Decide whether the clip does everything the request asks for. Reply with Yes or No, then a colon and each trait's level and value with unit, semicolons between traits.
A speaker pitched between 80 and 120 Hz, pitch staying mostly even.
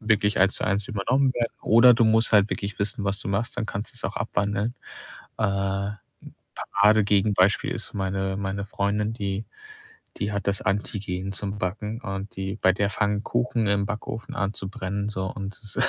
Yes: low, 100 Hz; narrow, 1.6 semitones